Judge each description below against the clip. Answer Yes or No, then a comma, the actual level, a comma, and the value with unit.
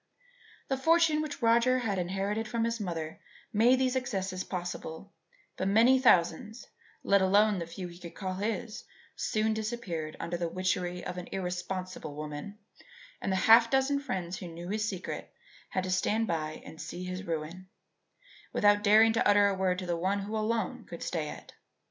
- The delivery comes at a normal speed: Yes, average, 175 wpm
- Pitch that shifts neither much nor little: Yes, average, 4.0 semitones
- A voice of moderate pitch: No, high, 195 Hz